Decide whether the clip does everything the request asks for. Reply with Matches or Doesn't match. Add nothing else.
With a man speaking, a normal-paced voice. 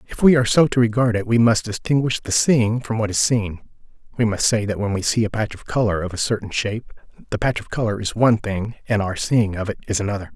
Doesn't match